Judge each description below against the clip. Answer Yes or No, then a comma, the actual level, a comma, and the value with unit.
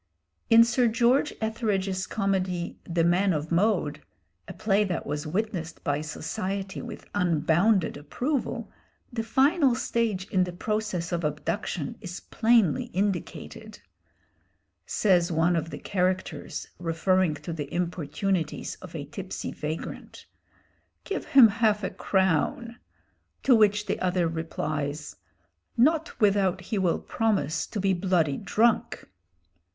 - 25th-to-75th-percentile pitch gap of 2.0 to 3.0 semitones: No, average, 4.6 semitones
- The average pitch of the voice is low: No, medium, 185 Hz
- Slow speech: Yes, slow, 125 wpm